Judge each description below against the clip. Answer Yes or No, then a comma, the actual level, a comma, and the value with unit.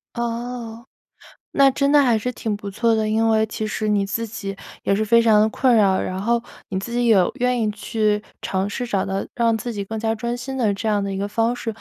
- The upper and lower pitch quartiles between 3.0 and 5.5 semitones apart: No, narrow, 2.6 semitones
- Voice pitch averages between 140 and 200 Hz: No, high, 220 Hz